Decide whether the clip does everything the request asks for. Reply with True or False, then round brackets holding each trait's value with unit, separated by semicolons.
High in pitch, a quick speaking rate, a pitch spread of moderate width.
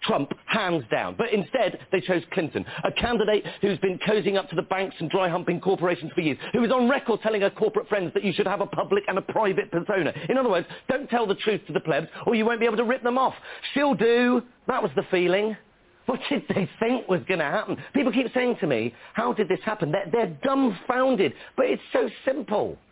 True (205 Hz; 235 wpm; 4.2 semitones)